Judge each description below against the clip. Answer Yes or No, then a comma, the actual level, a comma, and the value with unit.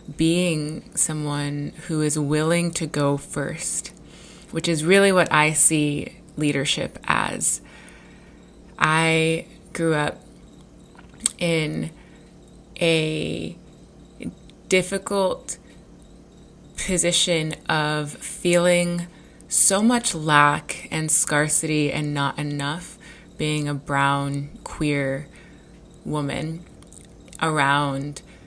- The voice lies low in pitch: No, medium, 155 Hz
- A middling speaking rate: No, slow, 80 wpm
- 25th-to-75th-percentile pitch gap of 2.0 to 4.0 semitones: Yes, average, 2.7 semitones